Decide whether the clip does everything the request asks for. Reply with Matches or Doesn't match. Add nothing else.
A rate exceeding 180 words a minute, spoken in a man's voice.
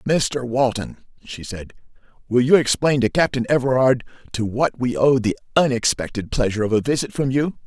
Doesn't match